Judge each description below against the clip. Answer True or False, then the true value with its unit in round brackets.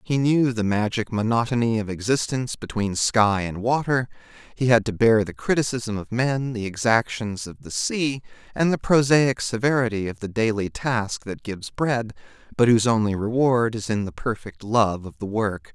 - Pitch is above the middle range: False (115 Hz)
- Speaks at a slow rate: False (175 wpm)